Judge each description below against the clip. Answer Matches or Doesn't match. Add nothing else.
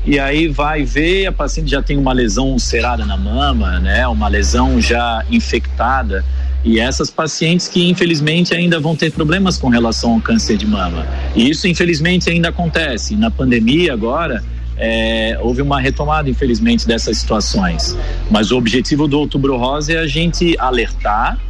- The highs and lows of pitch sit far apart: Matches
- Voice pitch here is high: Doesn't match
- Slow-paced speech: Doesn't match